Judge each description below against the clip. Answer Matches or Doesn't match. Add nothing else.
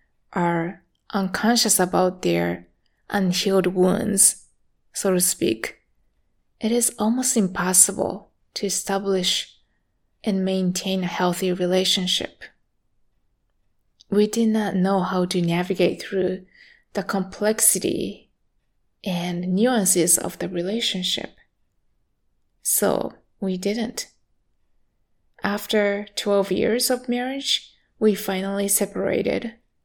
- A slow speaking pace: Matches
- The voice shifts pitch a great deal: Doesn't match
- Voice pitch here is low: Doesn't match